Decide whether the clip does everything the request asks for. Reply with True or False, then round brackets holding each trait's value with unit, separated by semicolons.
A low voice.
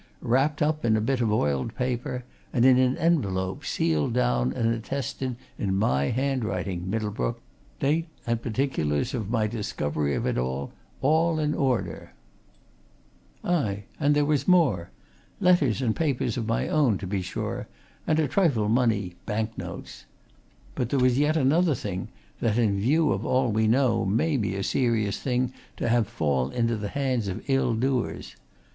True (115 Hz)